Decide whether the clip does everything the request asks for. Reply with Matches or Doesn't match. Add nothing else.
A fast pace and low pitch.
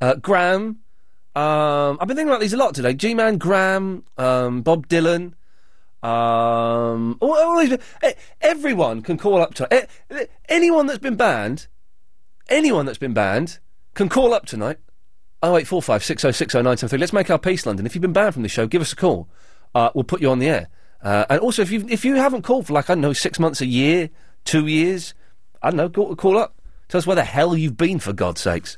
Doesn't match